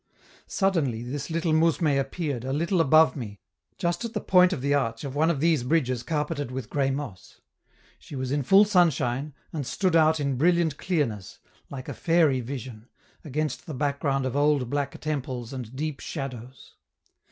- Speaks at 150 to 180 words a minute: Yes, average, 175 wpm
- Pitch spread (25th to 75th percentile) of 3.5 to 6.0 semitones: Yes, average, 3.8 semitones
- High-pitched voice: No, medium, 145 Hz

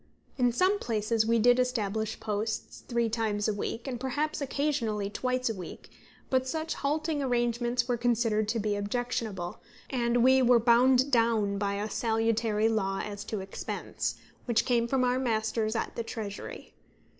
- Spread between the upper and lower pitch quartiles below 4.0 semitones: Yes, average, 2.7 semitones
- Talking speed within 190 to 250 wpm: No, average, 160 wpm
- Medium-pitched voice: No, high, 230 Hz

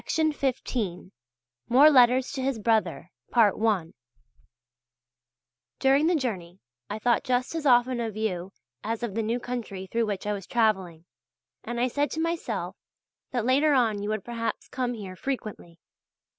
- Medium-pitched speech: No, high, 225 Hz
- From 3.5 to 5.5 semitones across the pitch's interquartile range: Yes, average, 5.0 semitones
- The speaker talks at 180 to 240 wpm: No, average, 145 wpm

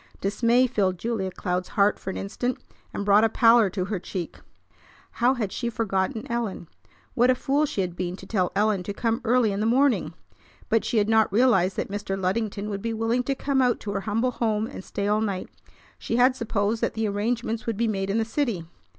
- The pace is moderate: No, fast, 220 wpm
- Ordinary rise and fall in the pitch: Yes, average, 3.2 semitones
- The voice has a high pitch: Yes, high, 220 Hz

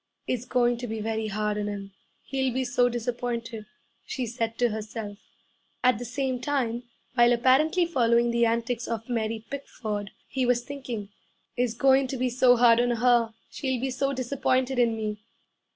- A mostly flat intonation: Yes, narrow, 2.2 semitones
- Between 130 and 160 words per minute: No, average, 170 wpm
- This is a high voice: Yes, high, 240 Hz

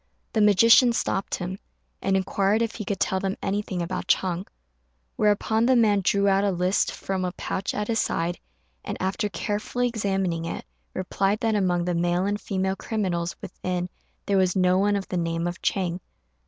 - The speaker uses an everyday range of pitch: No, narrow, 2.3 semitones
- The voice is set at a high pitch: Yes, high, 195 Hz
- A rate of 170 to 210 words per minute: Yes, average, 180 wpm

